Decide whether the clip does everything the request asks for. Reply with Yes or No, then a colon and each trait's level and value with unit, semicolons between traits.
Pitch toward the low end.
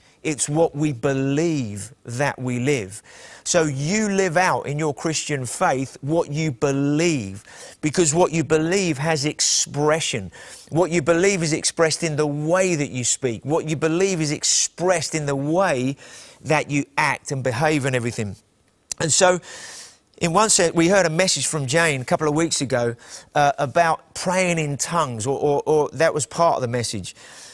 No: medium, 150 Hz